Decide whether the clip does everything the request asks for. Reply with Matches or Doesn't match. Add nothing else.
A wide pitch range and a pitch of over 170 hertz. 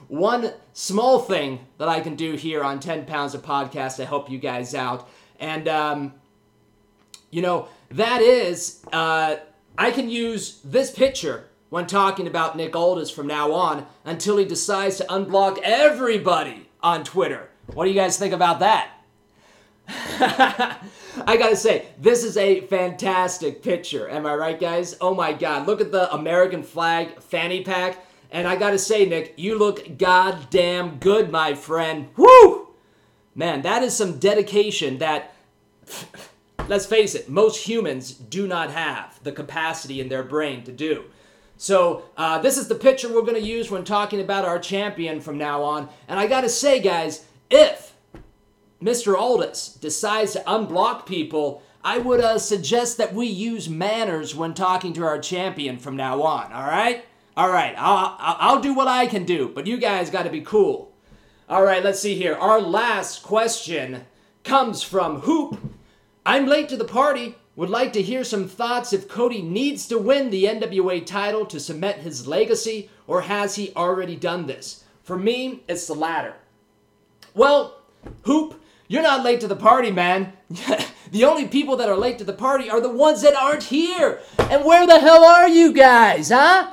Matches